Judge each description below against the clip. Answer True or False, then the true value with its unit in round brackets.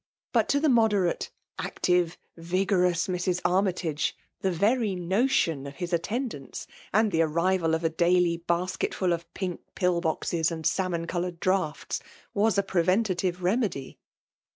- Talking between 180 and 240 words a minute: False (140 wpm)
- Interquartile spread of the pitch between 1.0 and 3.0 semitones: True (2.5 semitones)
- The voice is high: False (180 Hz)